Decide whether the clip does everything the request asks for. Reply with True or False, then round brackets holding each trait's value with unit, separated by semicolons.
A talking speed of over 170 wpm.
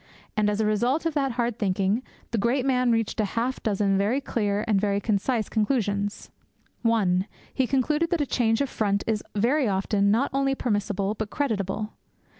True (180 wpm)